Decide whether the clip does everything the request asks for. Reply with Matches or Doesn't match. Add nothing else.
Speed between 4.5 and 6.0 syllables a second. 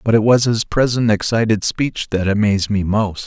Matches